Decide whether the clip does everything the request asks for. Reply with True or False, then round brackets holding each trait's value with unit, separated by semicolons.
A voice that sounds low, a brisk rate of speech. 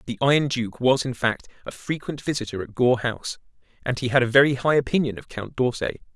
True (125 Hz; 215 wpm)